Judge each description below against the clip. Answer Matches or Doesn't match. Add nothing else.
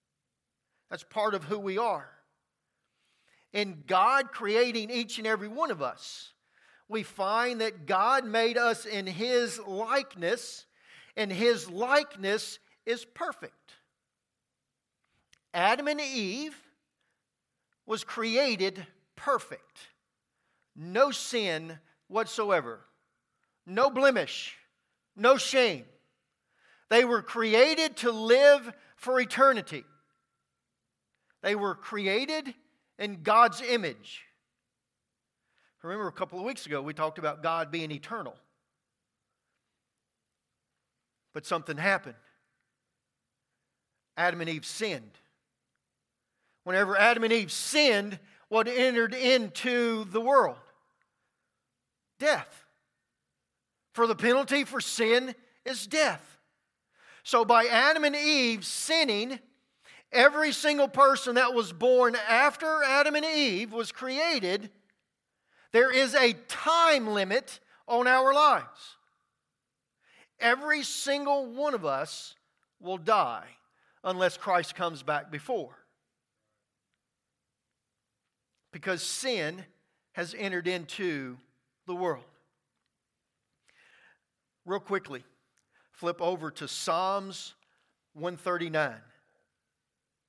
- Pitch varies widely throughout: Matches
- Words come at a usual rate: Doesn't match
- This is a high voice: Matches